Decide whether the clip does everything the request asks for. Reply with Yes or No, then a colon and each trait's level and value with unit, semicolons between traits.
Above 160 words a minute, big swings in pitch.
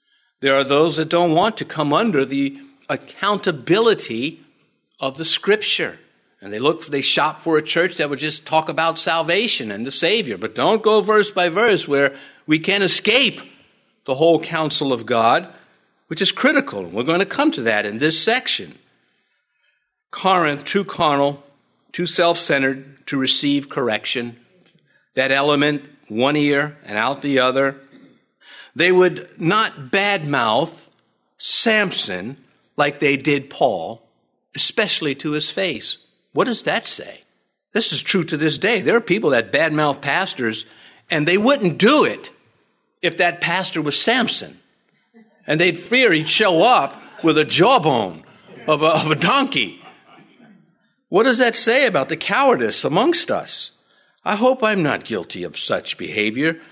No: average, 155 wpm; wide, 6.3 semitones